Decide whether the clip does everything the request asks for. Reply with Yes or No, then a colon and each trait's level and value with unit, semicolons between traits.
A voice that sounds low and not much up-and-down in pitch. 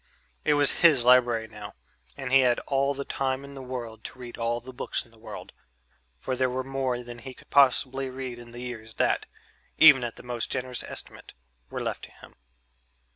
Yes: low, 125 Hz; narrow, 2.0 semitones